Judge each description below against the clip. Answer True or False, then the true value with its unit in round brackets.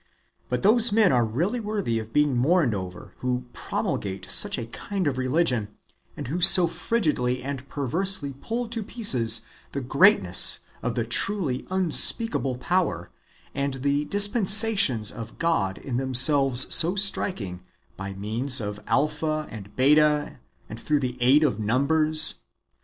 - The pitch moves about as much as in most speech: False (6.9 semitones)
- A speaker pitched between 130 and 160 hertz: True (140 Hz)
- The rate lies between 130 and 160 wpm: True (140 wpm)